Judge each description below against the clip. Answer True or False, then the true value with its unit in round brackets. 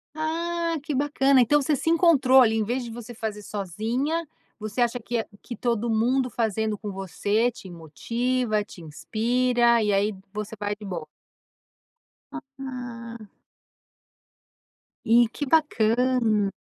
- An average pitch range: True (3.7 semitones)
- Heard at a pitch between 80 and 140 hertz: False (235 Hz)